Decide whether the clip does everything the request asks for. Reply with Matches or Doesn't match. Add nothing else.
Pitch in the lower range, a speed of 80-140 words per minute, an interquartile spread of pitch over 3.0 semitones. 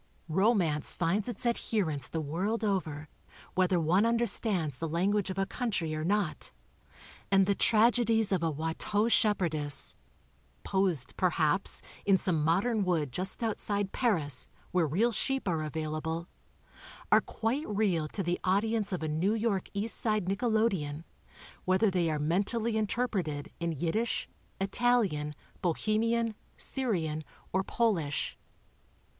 Doesn't match